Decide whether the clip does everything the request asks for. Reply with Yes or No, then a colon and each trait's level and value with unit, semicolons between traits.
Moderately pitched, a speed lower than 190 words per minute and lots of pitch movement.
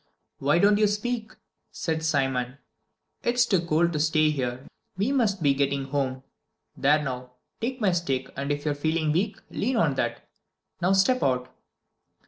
Yes: medium, 155 Hz; average, 160 wpm; wide, 6.7 semitones